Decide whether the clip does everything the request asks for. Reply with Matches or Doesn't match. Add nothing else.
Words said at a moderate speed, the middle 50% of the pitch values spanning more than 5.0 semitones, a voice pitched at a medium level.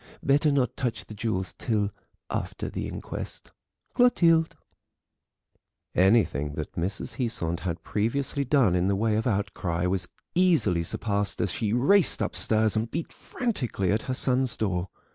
Doesn't match